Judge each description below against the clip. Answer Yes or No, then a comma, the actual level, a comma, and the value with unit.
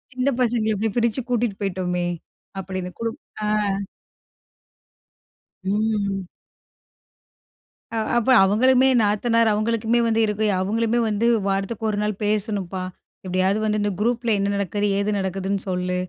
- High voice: Yes, high, 210 Hz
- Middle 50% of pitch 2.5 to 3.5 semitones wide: Yes, average, 2.8 semitones